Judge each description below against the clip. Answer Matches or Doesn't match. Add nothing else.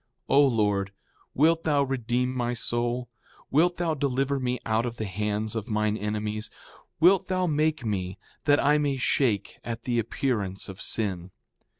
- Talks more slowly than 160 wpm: Doesn't match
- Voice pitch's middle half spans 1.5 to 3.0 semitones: Doesn't match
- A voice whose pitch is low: Matches